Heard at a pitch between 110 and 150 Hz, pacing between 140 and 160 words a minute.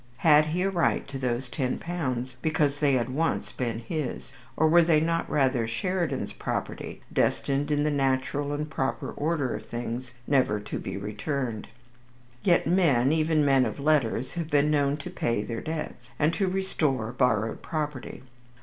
No: medium, 140 Hz; average, 170 wpm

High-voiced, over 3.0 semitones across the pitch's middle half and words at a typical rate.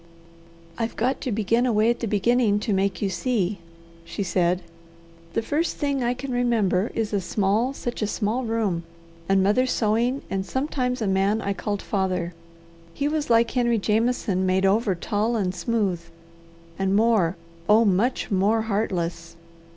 Yes: high, 215 Hz; average, 3.7 semitones; average, 160 wpm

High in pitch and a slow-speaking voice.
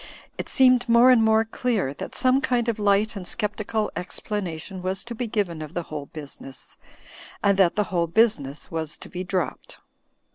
No: high, 200 Hz; average, 185 wpm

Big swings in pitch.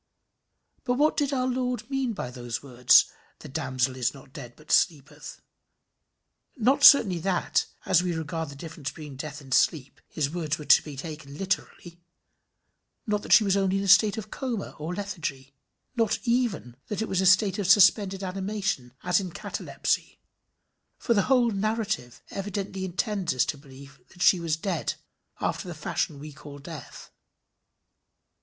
Yes: wide, 6.3 semitones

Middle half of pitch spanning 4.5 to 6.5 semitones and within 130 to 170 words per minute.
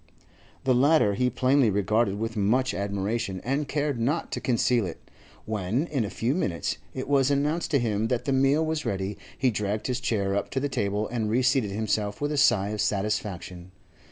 No: average, 4.8 semitones; average, 190 wpm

